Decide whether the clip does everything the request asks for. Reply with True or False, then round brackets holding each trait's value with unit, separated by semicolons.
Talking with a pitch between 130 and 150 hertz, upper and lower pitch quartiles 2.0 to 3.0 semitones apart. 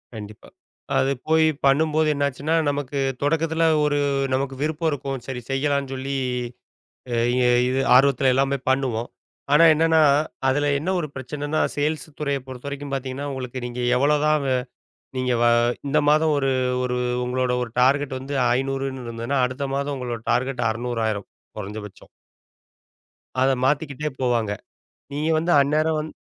True (135 Hz; 2.6 semitones)